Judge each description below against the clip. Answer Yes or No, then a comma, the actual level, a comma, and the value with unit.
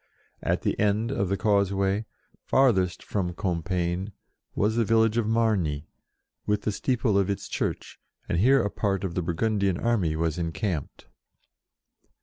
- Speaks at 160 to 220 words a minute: No, average, 145 wpm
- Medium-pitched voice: No, low, 100 Hz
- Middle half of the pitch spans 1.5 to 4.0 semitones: Yes, average, 3.7 semitones